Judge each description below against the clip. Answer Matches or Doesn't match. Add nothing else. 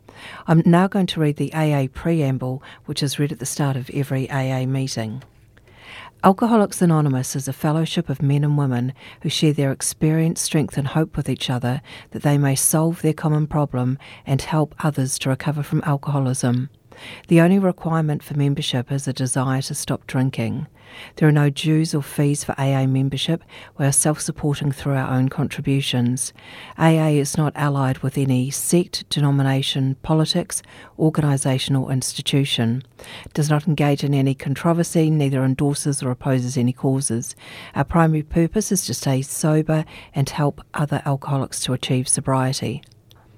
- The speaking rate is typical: Matches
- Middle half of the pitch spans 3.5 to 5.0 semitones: Doesn't match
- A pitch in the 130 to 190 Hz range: Matches